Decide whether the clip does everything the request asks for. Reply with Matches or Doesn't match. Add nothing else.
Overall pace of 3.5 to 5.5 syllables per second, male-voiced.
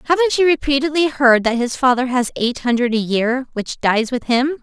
Doesn't match